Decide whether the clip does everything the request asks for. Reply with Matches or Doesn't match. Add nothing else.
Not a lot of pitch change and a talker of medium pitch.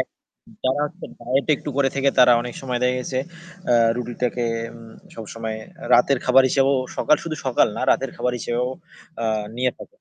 Doesn't match